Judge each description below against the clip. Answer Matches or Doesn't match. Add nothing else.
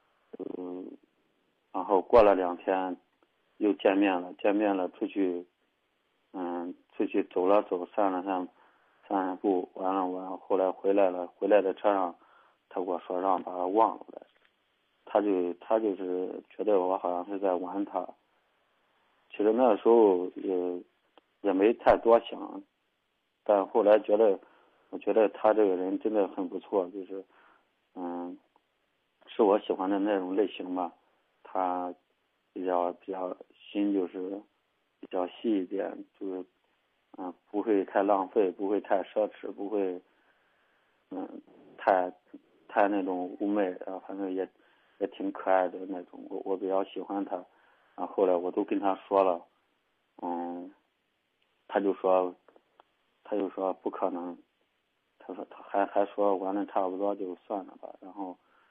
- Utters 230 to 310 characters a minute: Doesn't match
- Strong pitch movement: Doesn't match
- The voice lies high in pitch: Doesn't match